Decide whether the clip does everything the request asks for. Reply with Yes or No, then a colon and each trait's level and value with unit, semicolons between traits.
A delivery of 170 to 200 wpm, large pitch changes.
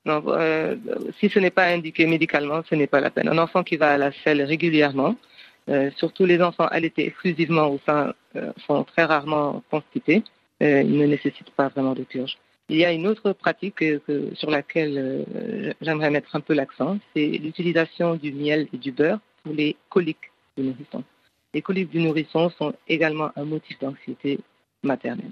No: average, 185 wpm; narrow, 2.5 semitones